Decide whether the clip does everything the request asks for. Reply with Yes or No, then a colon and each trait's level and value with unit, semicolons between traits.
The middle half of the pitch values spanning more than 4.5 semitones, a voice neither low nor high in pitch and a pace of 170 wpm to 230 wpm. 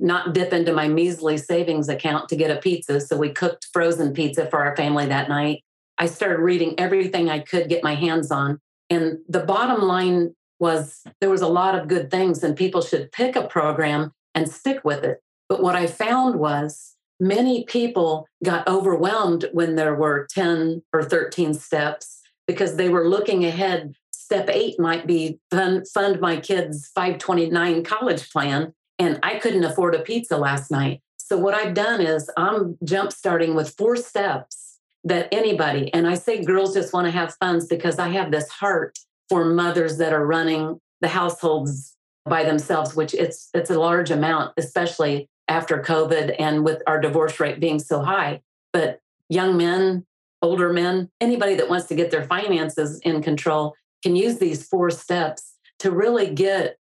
No: average, 2.8 semitones; medium, 170 Hz; average, 175 wpm